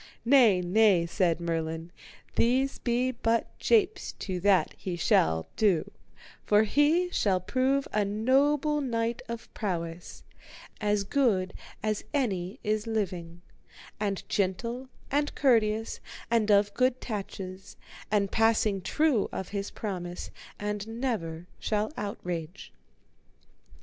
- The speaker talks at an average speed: No, slow, 115 wpm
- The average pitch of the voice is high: Yes, high, 210 Hz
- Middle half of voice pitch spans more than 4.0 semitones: Yes, average, 4.6 semitones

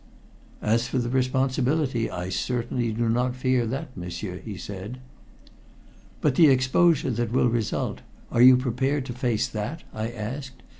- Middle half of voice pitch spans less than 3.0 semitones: Yes, narrow, 2.6 semitones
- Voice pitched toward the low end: Yes, low, 125 Hz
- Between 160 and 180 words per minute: No, average, 150 wpm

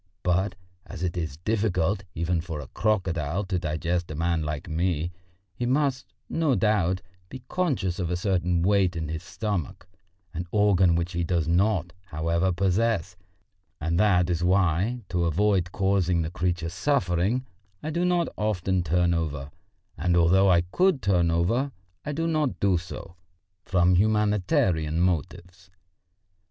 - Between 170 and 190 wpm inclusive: No, average, 150 wpm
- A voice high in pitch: No, very low, 90 Hz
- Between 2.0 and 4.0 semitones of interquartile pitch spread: Yes, average, 3.5 semitones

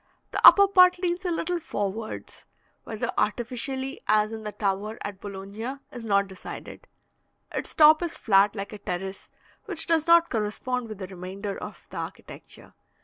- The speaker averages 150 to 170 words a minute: Yes, average, 160 wpm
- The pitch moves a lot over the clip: Yes, wide, 7.7 semitones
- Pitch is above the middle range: Yes, high, 220 Hz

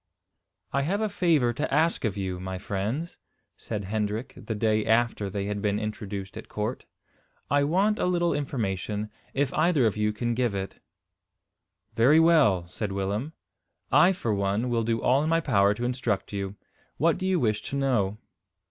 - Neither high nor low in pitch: No, low, 115 Hz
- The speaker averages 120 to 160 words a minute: No, average, 175 wpm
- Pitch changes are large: Yes, wide, 5.9 semitones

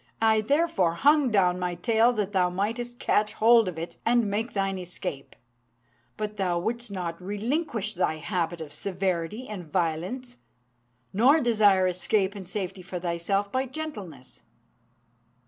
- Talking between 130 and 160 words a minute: Yes, average, 145 wpm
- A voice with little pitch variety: No, average, 4.3 semitones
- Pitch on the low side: No, high, 200 Hz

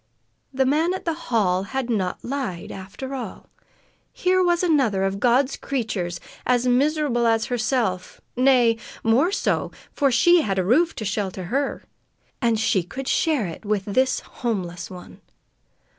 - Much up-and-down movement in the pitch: Yes, wide, 5.8 semitones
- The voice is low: No, high, 240 Hz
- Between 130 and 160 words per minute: Yes, average, 150 wpm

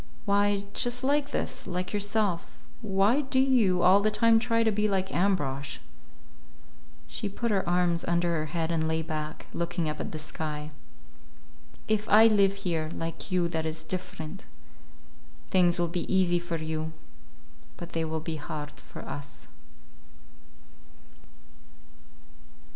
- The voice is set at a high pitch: No, medium, 175 Hz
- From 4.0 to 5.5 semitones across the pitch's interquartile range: Yes, average, 4.3 semitones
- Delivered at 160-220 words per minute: No, average, 140 wpm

